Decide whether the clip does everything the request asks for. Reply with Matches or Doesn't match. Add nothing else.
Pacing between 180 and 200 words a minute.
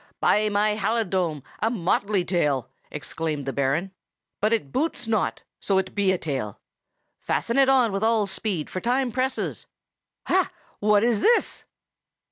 Doesn't match